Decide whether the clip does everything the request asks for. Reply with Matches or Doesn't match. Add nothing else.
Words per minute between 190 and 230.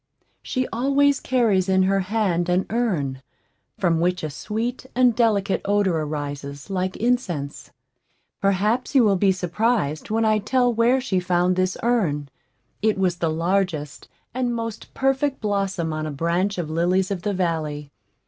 Doesn't match